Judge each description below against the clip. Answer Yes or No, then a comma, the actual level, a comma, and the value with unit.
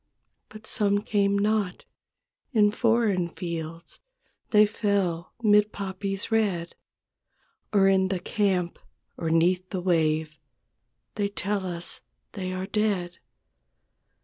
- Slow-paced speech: Yes, slow, 110 wpm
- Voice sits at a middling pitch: No, high, 195 Hz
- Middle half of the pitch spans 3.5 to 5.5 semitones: No, average, 2.9 semitones